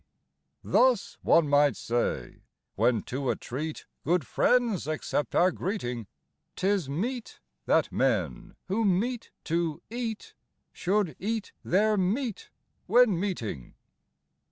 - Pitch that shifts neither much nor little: No, wide, 7.0 semitones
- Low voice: No, medium, 185 Hz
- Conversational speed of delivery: No, slow, 110 wpm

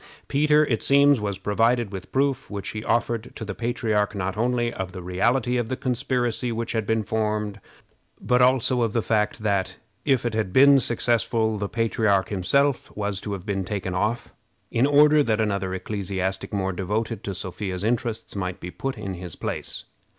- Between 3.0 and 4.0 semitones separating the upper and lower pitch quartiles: Yes, average, 3.6 semitones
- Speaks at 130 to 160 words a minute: No, average, 180 wpm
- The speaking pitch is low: Yes, low, 110 Hz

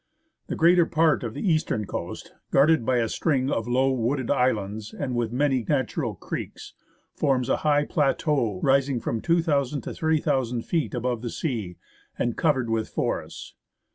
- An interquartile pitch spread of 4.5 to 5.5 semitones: No, average, 3.9 semitones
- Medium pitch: No, low, 130 Hz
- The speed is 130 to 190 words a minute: Yes, average, 160 wpm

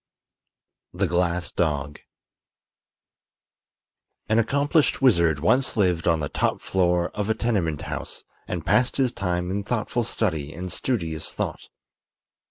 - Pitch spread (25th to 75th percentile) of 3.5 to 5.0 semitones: No, wide, 5.4 semitones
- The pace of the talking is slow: Yes, slow, 125 wpm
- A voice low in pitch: Yes, very low, 90 Hz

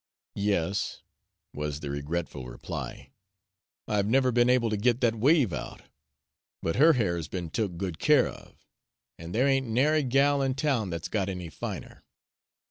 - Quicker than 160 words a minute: No, average, 155 wpm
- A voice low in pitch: Yes, low, 110 Hz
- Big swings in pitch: Yes, wide, 7.2 semitones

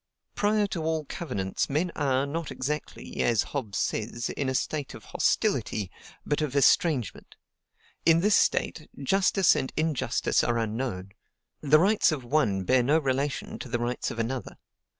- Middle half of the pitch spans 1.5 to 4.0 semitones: No, average, 4.9 semitones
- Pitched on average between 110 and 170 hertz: Yes, medium, 140 Hz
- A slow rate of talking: No, average, 155 wpm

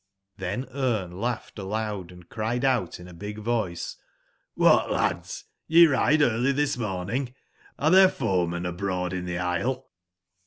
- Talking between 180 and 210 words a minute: No, average, 155 wpm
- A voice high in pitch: No, low, 110 Hz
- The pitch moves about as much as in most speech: No, wide, 6.2 semitones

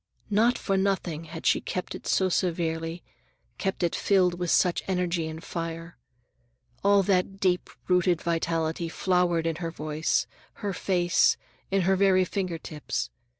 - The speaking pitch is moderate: Yes, medium, 175 Hz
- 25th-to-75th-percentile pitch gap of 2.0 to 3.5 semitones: Yes, narrow, 2.4 semitones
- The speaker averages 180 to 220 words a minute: No, average, 150 wpm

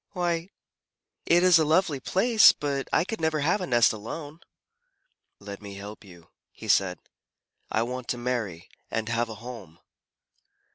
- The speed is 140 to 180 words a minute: Yes, average, 155 wpm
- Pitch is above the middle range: No, low, 125 Hz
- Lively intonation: Yes, wide, 7.6 semitones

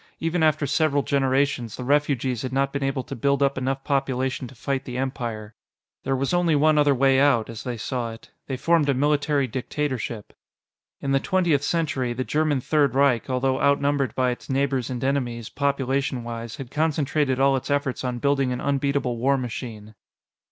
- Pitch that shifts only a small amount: Yes, narrow, 2.1 semitones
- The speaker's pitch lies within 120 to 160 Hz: Yes, low, 135 Hz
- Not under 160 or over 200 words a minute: Yes, average, 180 wpm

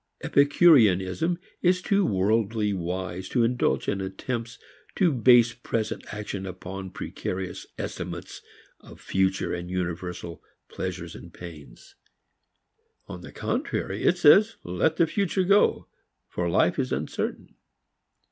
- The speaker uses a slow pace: Yes, slow, 120 wpm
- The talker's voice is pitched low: Yes, low, 100 Hz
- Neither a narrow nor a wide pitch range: No, wide, 7.5 semitones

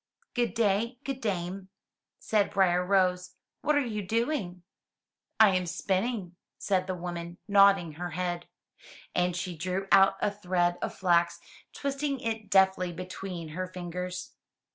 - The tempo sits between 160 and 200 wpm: No, average, 140 wpm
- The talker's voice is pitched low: No, medium, 185 Hz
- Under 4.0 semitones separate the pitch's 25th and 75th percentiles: Yes, narrow, 2.6 semitones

